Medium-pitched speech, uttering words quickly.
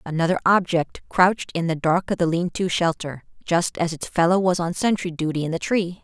Yes: medium, 170 Hz; fast, 220 wpm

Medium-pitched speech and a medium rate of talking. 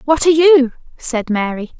No: very high, 270 Hz; average, 170 wpm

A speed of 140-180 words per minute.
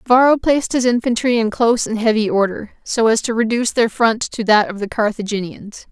No: fast, 205 wpm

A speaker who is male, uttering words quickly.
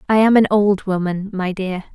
No: female; fast, 215 wpm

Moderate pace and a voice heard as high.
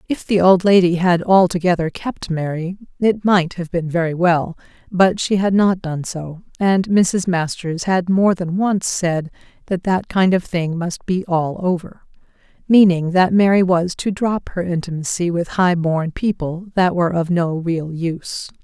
No: average, 175 wpm; medium, 180 Hz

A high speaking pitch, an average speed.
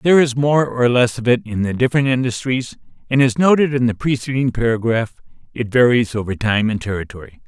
No: low, 120 Hz; average, 195 wpm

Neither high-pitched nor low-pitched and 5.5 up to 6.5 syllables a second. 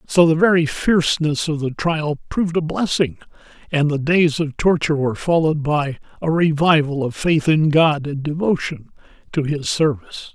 No: medium, 155 Hz; 5.1 syllables/s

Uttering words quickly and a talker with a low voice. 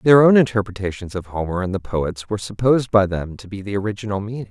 Yes: fast, 225 wpm; low, 105 Hz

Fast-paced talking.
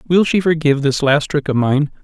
Yes: fast, 235 wpm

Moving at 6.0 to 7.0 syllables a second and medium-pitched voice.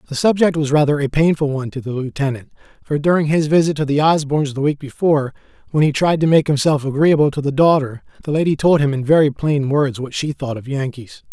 Yes: 6.1 syllables/s; medium, 145 Hz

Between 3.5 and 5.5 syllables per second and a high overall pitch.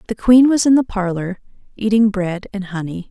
Yes: 5.1 syllables/s; high, 205 Hz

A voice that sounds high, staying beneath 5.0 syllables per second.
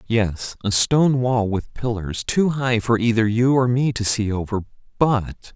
No: low, 115 Hz; 4.2 syllables/s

